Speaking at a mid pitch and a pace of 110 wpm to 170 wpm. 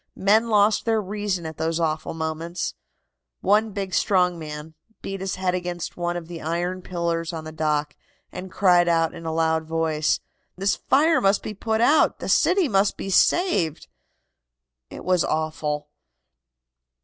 Yes: medium, 175 Hz; average, 160 wpm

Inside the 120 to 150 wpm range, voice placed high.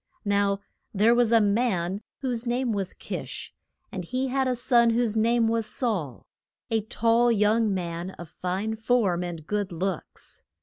No: average, 160 wpm; high, 220 Hz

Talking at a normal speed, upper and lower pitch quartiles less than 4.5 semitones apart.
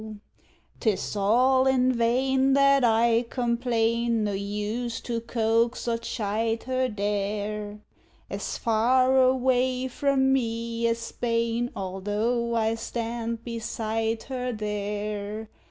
No: slow, 105 wpm; narrow, 2.4 semitones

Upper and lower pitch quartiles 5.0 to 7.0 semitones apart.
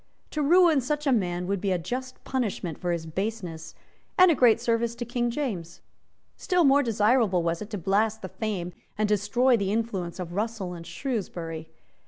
Yes: wide, 5.6 semitones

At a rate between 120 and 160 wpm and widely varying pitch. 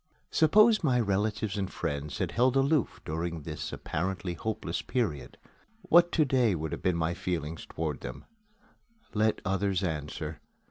Yes: average, 140 wpm; wide, 7.1 semitones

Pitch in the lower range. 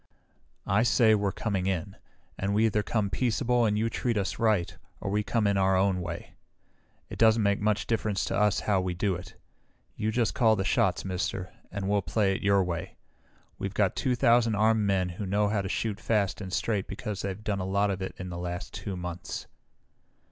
Yes: low, 100 Hz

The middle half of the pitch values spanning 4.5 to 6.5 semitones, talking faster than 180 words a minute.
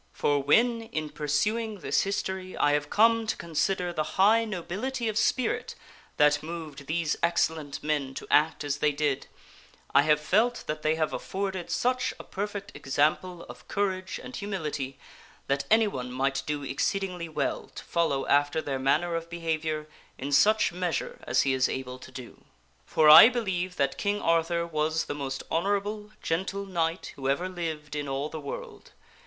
No: average, 5.0 semitones; average, 170 wpm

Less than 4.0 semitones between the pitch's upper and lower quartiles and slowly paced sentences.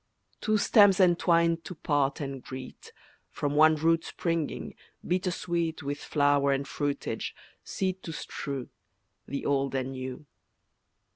Yes: average, 3.4 semitones; slow, 130 wpm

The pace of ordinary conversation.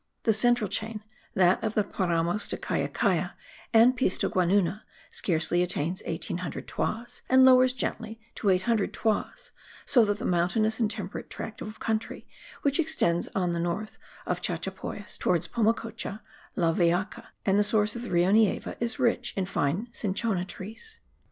Yes: average, 150 wpm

